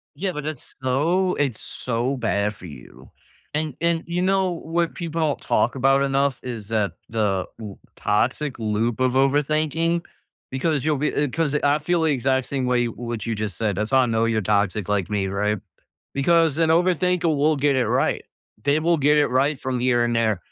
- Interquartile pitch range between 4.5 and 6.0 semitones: Yes, wide, 5.5 semitones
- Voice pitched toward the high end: No, low, 135 Hz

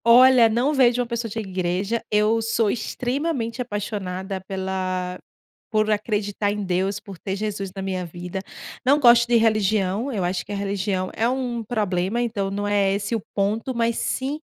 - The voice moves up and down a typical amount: Yes, average, 3.4 semitones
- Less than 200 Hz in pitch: No, high, 210 Hz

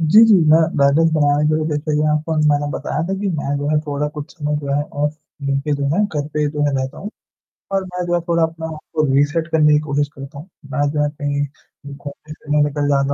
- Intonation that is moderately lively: No, narrow, 1.6 semitones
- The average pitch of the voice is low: No, medium, 150 Hz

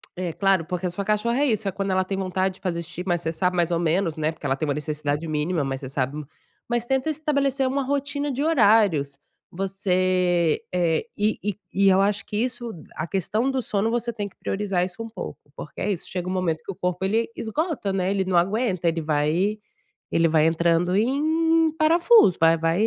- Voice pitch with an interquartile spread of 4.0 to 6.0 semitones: Yes, average, 4.8 semitones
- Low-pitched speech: No, high, 190 Hz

